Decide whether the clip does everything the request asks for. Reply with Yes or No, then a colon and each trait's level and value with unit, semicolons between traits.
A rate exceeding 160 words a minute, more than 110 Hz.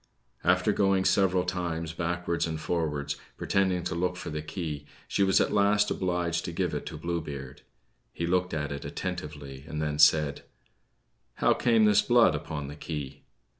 No: average, 170 wpm; very low, 85 Hz